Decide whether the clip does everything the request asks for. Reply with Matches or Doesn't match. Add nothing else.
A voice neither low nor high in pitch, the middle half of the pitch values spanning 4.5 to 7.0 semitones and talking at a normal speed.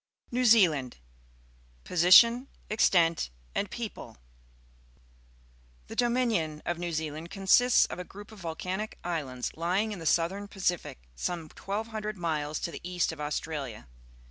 Doesn't match